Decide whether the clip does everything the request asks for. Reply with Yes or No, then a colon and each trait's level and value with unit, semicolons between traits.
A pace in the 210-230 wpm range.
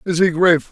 No: fast, 250 wpm